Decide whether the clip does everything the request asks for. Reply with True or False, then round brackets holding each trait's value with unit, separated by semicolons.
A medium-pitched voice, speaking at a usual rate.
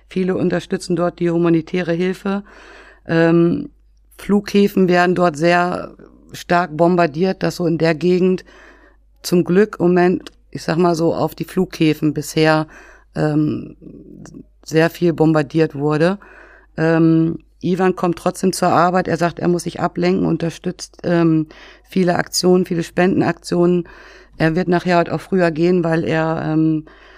True (170 Hz; 135 wpm)